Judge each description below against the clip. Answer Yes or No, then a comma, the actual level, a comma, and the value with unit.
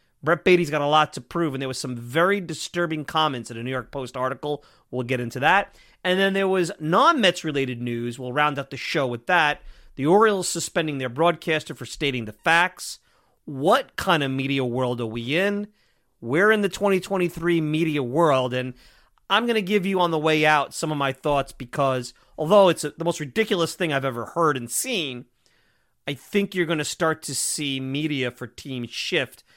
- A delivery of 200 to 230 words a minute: Yes, fast, 205 wpm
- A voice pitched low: No, medium, 150 Hz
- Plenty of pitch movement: No, average, 4.9 semitones